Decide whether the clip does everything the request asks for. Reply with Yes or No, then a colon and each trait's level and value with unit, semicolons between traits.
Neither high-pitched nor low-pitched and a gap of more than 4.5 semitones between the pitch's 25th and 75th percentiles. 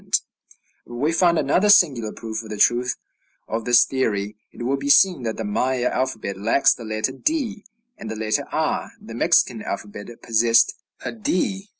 No: low, 120 Hz; wide, 5.6 semitones